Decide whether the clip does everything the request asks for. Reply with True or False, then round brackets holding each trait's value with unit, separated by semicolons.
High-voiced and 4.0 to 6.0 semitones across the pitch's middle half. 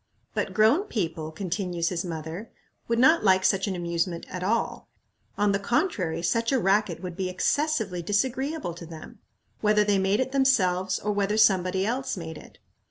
True (195 Hz; 4.4 semitones)